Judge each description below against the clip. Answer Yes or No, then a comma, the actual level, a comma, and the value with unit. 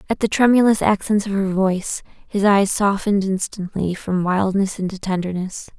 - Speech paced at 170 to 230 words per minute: No, average, 155 wpm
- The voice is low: No, high, 195 Hz